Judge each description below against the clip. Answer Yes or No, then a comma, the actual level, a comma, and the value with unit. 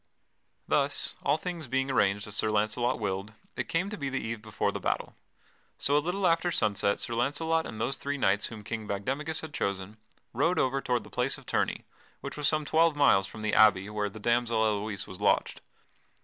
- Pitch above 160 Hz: No, low, 120 Hz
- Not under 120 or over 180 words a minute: No, fast, 205 wpm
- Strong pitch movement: Yes, wide, 5.7 semitones